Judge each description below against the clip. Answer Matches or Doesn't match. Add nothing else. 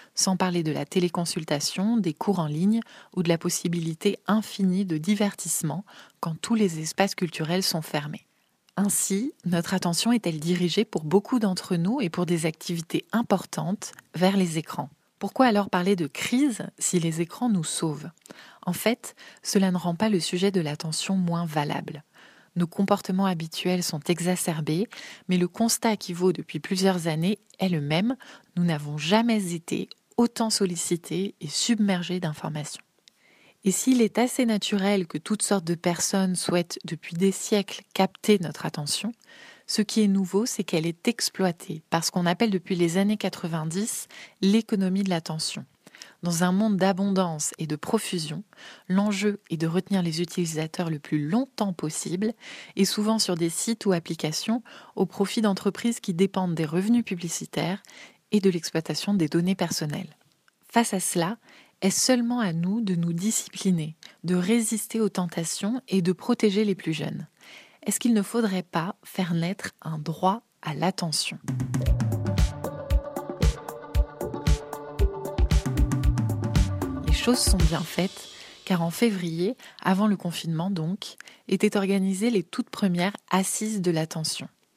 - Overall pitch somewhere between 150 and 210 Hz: Matches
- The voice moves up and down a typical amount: Matches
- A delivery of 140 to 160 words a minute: Matches